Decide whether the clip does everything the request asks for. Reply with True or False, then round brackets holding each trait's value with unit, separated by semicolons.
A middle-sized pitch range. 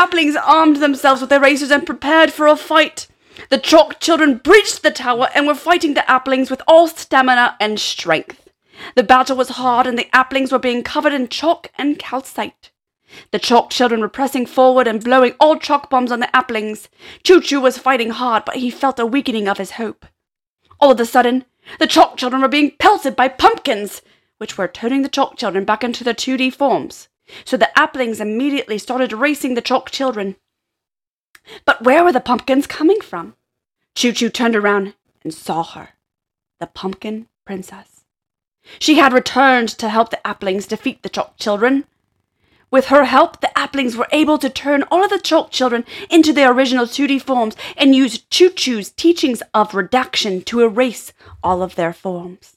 True (3.8 semitones)